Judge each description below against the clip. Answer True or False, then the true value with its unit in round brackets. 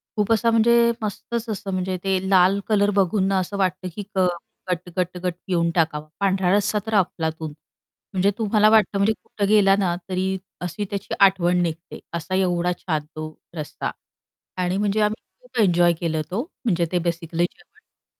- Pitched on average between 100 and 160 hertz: False (190 Hz)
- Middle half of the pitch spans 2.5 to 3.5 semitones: True (2.9 semitones)